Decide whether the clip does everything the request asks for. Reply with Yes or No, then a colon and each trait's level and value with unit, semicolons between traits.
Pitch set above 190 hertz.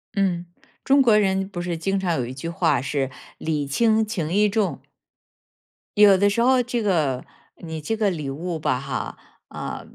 No: medium, 185 Hz